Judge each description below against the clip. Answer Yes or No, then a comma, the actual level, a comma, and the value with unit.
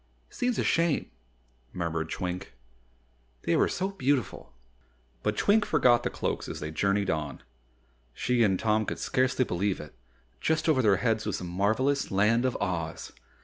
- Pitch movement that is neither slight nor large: No, wide, 6.2 semitones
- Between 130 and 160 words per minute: Yes, average, 155 wpm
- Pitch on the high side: No, low, 110 Hz